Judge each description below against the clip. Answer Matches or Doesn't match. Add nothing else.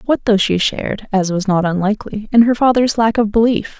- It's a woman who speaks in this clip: Matches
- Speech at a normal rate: Matches